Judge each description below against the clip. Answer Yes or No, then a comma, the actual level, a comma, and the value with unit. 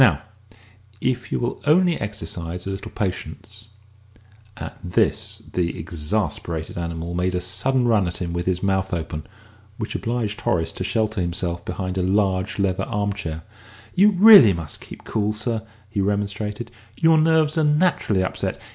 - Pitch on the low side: Yes, low, 100 Hz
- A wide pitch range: No, average, 4.1 semitones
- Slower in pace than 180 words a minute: Yes, average, 160 wpm